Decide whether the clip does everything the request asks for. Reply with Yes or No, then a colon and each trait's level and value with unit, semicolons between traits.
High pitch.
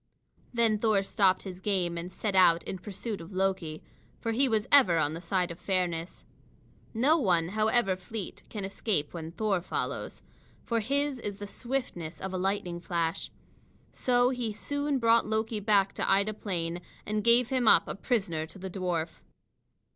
Yes: high, 195 Hz